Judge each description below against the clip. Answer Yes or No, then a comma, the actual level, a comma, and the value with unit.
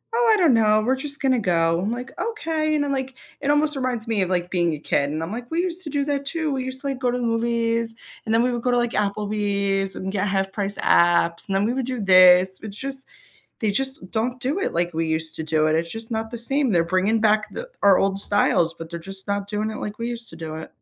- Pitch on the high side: Yes, high, 220 Hz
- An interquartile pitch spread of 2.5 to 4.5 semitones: No, wide, 5.4 semitones